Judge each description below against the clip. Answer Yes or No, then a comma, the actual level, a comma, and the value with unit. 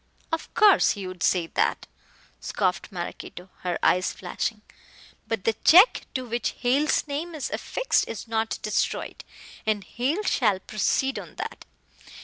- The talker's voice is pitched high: Yes, high, 225 Hz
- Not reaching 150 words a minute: Yes, average, 140 wpm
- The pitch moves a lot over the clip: Yes, wide, 7.0 semitones